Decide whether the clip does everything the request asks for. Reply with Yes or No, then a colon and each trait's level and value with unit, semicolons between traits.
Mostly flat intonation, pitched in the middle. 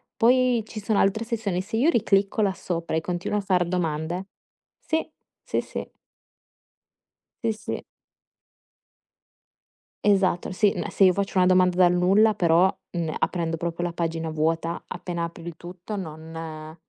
No: average, 3.4 semitones; medium, 180 Hz